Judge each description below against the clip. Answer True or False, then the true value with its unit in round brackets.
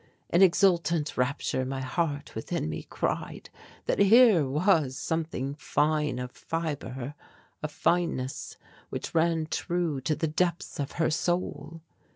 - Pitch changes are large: False (3.5 semitones)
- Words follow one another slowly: True (130 wpm)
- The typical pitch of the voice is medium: True (155 Hz)